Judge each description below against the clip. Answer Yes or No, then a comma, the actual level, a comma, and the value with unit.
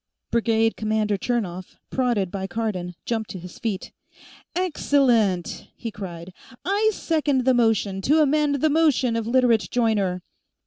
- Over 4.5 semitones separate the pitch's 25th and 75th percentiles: Yes, average, 5.1 semitones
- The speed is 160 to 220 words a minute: No, slow, 135 wpm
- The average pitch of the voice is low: No, high, 225 Hz